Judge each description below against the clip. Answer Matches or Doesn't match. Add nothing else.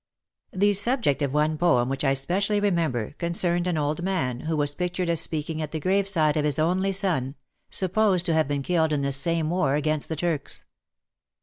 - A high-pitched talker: Doesn't match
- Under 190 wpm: Doesn't match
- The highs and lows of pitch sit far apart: Doesn't match